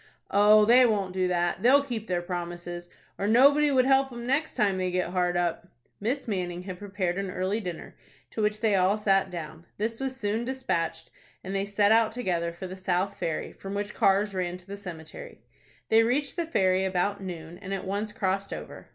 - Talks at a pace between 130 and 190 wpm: No, fast, 205 wpm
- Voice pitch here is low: No, high, 195 Hz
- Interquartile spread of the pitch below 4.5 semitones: Yes, average, 3.5 semitones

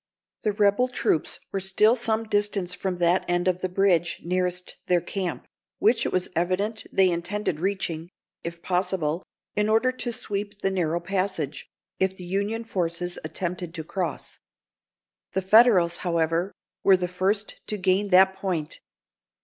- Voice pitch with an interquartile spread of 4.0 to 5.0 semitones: No, narrow, 2.6 semitones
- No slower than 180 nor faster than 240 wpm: No, average, 150 wpm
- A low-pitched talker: No, medium, 185 Hz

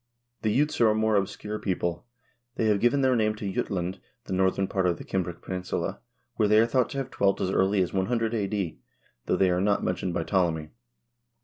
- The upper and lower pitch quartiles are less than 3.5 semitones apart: Yes, average, 3.0 semitones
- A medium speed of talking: No, fast, 210 wpm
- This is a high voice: No, low, 100 Hz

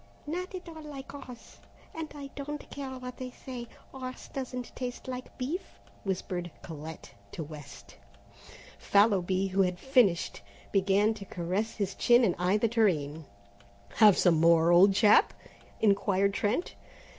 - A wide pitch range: Yes, wide, 6.0 semitones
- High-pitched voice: Yes, high, 210 Hz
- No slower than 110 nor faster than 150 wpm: Yes, average, 145 wpm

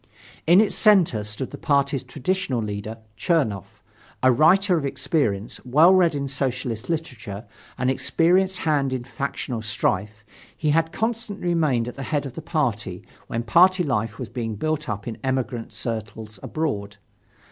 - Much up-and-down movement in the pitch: Yes, wide, 6.3 semitones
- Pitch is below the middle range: Yes, low, 130 Hz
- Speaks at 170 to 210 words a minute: No, average, 155 wpm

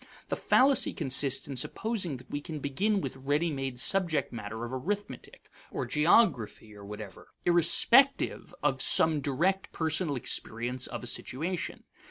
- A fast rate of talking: No, average, 145 wpm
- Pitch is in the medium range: Yes, medium, 145 Hz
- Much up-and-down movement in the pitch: Yes, wide, 6.3 semitones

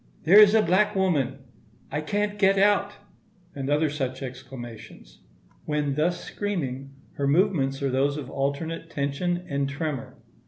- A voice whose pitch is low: No, medium, 150 Hz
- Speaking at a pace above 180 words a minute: No, average, 140 wpm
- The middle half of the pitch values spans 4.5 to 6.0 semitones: Yes, wide, 5.4 semitones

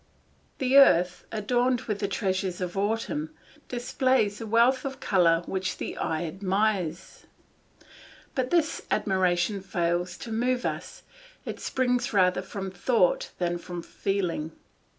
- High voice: Yes, high, 200 Hz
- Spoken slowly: Yes, slow, 130 wpm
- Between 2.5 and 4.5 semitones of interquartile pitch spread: No, average, 5.3 semitones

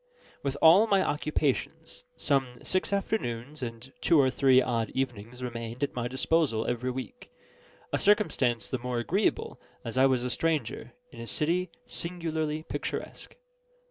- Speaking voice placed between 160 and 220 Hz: No, low, 130 Hz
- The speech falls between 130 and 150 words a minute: Yes, average, 145 wpm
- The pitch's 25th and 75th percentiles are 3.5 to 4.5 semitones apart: No, average, 5.1 semitones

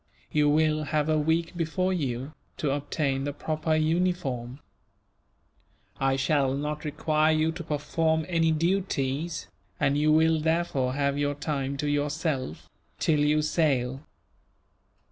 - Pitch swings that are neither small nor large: No, narrow, 2.3 semitones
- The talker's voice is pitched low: No, medium, 150 Hz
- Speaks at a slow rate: Yes, slow, 130 wpm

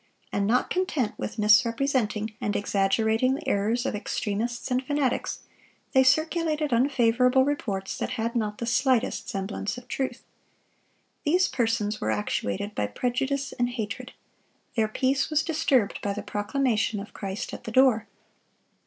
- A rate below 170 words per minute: Yes, average, 145 wpm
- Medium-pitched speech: No, high, 235 Hz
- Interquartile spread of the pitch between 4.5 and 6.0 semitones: No, average, 4.0 semitones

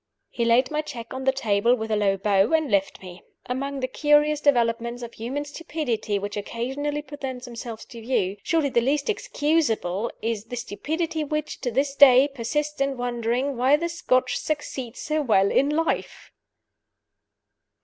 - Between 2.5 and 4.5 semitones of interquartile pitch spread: Yes, average, 4.1 semitones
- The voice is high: Yes, very high, 255 Hz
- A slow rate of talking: No, average, 165 wpm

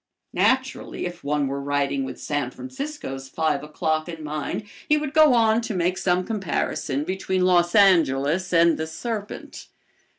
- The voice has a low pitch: No, medium, 175 Hz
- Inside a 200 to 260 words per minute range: No, average, 155 wpm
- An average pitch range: No, wide, 6.2 semitones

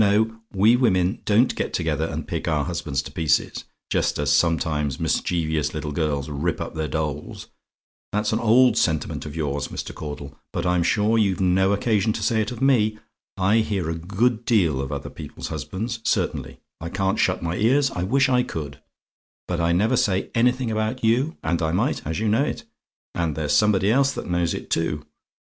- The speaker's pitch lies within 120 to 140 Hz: No, very low, 95 Hz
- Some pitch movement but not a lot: No, wide, 5.8 semitones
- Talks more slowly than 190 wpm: No, average, 195 wpm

